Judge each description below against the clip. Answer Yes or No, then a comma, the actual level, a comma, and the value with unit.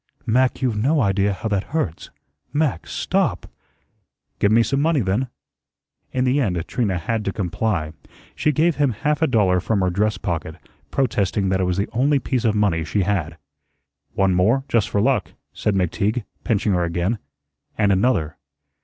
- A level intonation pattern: No, average, 5.3 semitones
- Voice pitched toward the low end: Yes, low, 105 Hz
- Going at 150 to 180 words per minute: Yes, average, 170 wpm